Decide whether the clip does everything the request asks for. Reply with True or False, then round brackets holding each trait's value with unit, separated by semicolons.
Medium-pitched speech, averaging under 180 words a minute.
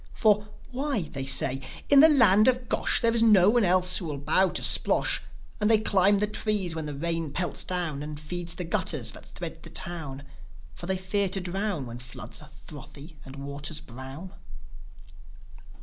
False (180 Hz; 190 wpm)